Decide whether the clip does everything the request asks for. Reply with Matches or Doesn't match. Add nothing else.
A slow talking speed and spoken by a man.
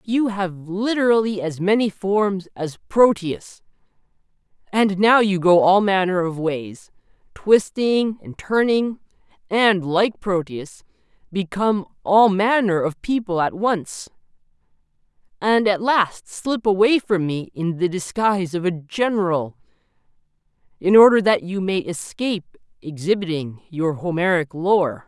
Matches